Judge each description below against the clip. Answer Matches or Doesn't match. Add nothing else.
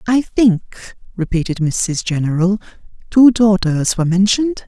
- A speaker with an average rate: Doesn't match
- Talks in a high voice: Matches